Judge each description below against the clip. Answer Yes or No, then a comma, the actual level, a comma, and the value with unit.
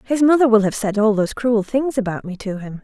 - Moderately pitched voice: No, high, 220 Hz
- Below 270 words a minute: No, fast, 275 wpm